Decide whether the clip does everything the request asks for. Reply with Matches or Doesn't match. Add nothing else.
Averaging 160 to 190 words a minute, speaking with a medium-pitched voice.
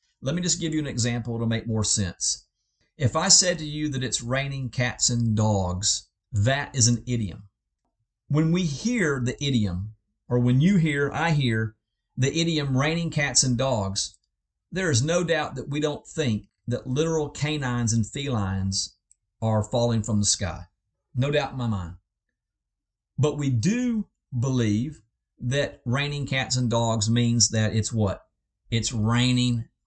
Doesn't match